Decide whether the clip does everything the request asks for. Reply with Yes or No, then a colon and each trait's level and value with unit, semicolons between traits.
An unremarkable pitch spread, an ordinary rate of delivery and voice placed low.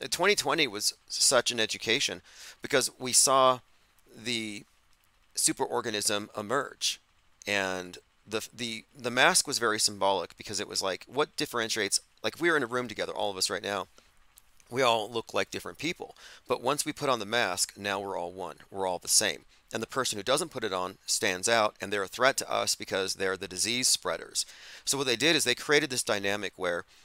Yes: average, 3.9 semitones; average, 195 wpm; low, 115 Hz